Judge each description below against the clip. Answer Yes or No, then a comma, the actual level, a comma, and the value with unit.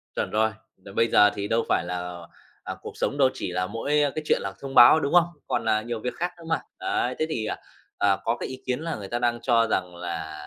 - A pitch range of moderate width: No, wide, 6.1 semitones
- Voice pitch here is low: Yes, low, 115 Hz